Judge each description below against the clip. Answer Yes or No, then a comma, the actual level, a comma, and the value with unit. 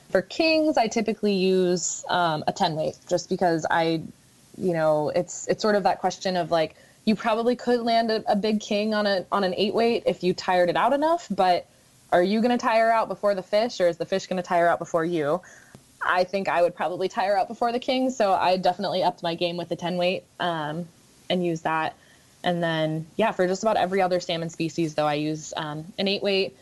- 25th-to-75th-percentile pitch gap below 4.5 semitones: Yes, average, 3.8 semitones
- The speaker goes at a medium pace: No, fast, 230 wpm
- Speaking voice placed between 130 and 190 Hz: Yes, medium, 185 Hz